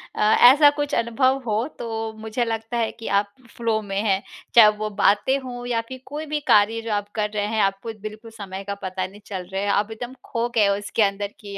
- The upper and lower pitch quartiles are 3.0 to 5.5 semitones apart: No, narrow, 2.6 semitones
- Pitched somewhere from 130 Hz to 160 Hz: No, high, 220 Hz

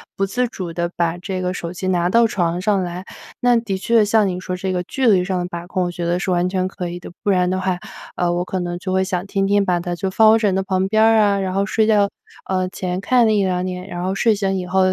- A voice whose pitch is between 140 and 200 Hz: Yes, medium, 185 Hz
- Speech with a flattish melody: Yes, narrow, 2.0 semitones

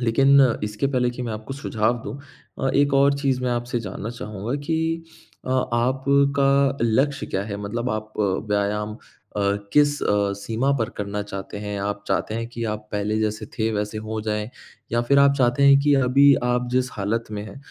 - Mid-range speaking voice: No, low, 115 Hz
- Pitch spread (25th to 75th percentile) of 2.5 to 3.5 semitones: No, average, 4.4 semitones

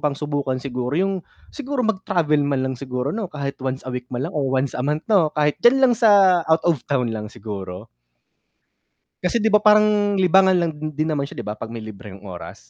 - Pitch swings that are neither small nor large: No, wide, 7.1 semitones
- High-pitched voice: No, medium, 150 Hz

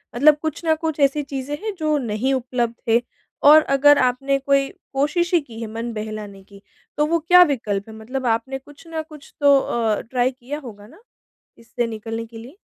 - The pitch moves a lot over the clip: No, average, 4.4 semitones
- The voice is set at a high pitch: Yes, very high, 265 Hz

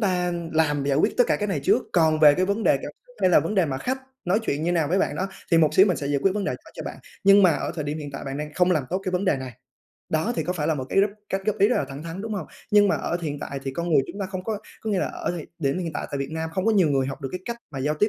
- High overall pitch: No, medium, 170 Hz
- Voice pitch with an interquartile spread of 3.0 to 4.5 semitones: No, average, 4.9 semitones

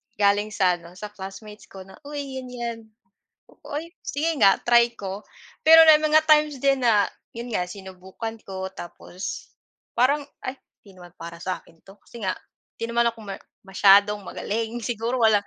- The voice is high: Yes, high, 215 Hz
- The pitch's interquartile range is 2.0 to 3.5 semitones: No, average, 4.6 semitones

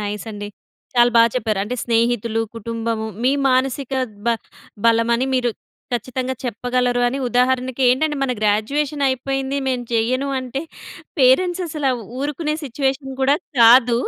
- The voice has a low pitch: No, very high, 250 Hz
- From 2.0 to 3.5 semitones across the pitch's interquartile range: Yes, narrow, 2.6 semitones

